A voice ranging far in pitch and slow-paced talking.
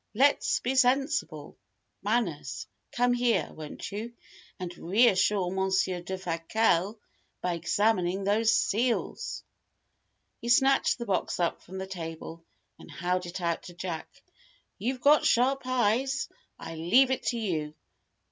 Yes: wide, 5.7 semitones; slow, 130 wpm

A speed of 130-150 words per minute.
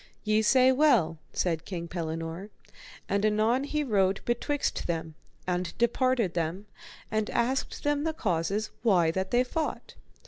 Yes: average, 140 wpm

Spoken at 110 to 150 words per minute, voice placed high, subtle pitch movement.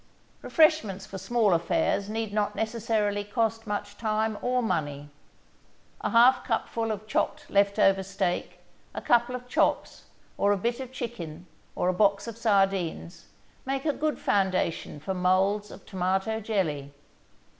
No: average, 145 wpm; high, 205 Hz; average, 3.2 semitones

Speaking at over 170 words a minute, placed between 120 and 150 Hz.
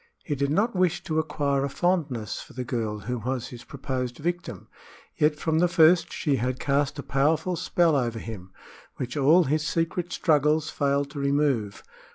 Yes: average, 180 wpm; medium, 140 Hz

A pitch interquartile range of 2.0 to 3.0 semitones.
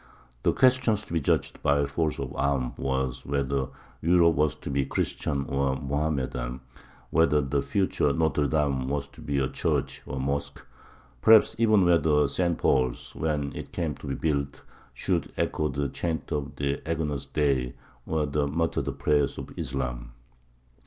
Yes: narrow, 2.6 semitones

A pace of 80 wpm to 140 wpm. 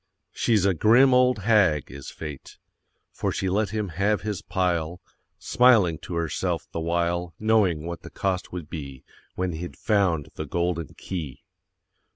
No: average, 155 wpm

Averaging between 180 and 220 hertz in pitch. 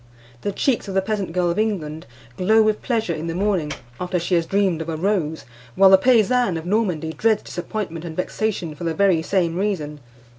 Yes: medium, 185 Hz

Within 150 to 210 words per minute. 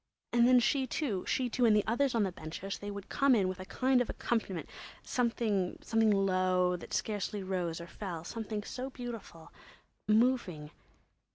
Yes: average, 155 wpm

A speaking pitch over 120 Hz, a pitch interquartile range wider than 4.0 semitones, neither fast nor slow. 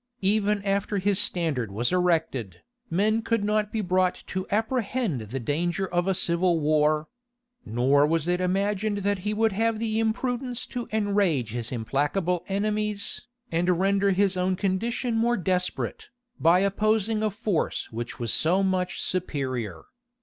Yes: high, 190 Hz; average, 4.5 semitones; average, 150 wpm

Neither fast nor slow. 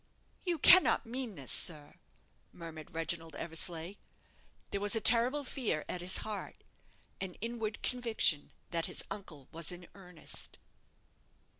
No: slow, 130 wpm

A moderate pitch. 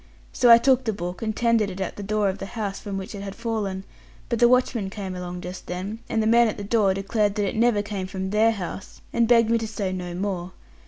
No: high, 205 Hz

